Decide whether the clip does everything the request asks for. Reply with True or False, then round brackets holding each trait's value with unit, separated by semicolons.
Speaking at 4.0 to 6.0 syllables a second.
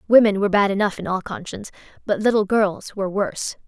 False (6.6 syllables/s)